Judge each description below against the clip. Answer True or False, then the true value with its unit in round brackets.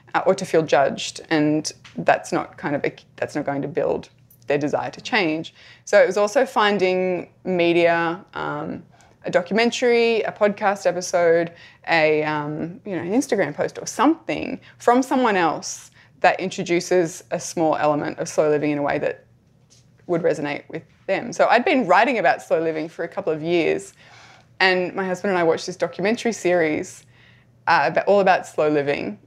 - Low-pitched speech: False (175 Hz)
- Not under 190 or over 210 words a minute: False (175 wpm)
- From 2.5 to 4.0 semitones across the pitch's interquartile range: True (3.7 semitones)